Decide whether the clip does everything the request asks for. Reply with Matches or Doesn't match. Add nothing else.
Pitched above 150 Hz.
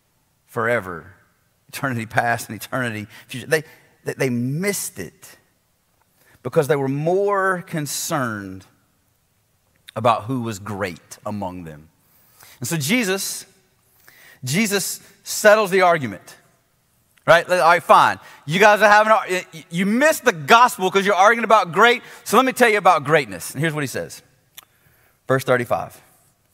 Doesn't match